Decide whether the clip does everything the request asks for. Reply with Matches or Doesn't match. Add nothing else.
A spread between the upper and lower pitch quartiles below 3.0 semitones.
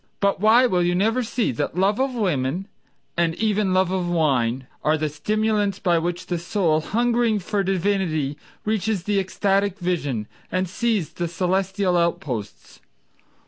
Doesn't match